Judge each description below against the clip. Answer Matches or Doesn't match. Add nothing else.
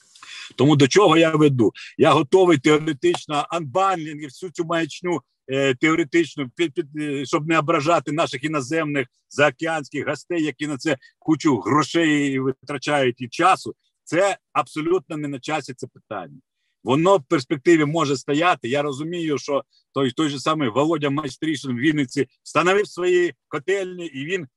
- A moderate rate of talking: Matches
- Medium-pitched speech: Matches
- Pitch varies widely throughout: Doesn't match